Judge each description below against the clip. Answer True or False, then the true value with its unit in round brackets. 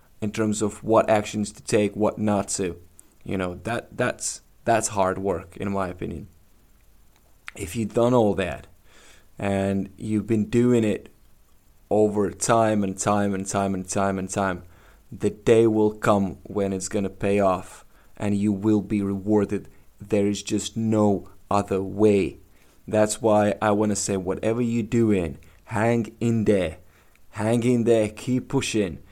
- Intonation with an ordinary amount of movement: False (1.9 semitones)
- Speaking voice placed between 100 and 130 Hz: True (105 Hz)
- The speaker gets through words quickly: False (155 wpm)